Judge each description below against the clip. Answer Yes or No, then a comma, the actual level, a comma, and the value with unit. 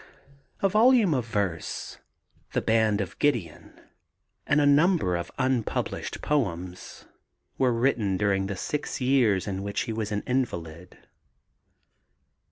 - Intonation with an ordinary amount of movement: No, wide, 6.0 semitones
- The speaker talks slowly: Yes, slow, 125 wpm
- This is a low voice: Yes, low, 110 Hz